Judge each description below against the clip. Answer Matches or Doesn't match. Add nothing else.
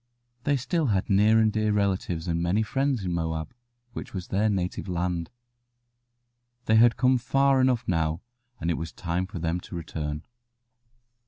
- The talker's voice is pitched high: Doesn't match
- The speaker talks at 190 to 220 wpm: Doesn't match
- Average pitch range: Matches